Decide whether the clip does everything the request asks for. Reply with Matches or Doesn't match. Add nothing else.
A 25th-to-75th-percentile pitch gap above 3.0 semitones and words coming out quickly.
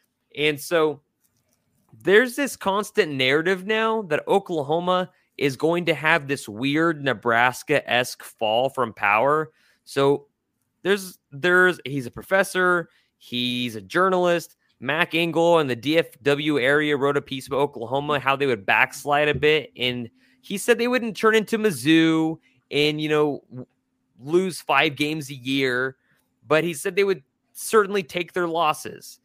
Doesn't match